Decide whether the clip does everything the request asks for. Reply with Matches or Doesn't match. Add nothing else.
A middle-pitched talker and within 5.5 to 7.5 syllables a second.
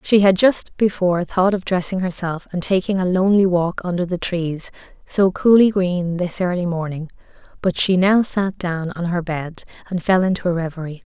Doesn't match